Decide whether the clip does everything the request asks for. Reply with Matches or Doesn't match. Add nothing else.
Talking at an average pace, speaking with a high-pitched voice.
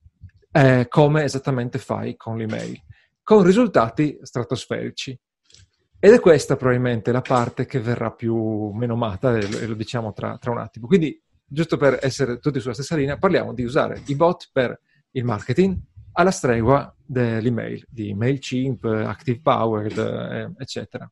Doesn't match